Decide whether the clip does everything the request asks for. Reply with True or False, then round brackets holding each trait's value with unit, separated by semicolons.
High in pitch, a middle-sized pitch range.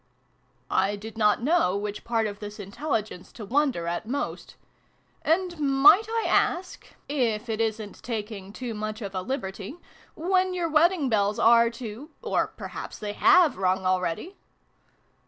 False (225 Hz; 6.4 semitones)